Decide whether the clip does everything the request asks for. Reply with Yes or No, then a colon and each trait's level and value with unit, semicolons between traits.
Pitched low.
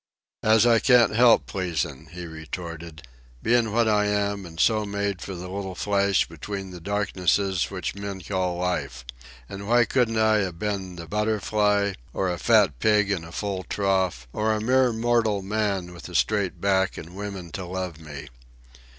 Yes: low, 100 Hz